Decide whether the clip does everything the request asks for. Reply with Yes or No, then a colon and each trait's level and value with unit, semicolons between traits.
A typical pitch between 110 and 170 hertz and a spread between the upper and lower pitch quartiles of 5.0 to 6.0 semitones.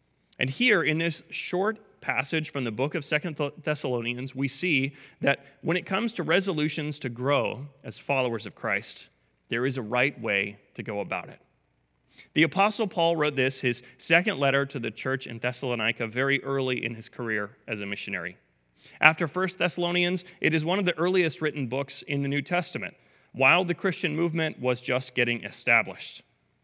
Yes: medium, 140 Hz; wide, 5.6 semitones